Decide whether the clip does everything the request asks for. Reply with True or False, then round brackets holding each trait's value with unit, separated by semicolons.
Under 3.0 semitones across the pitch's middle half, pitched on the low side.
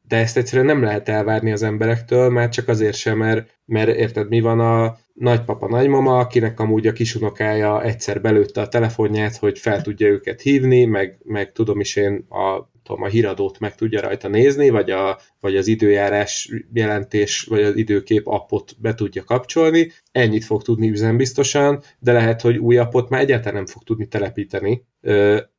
True (2.4 semitones; 110 Hz)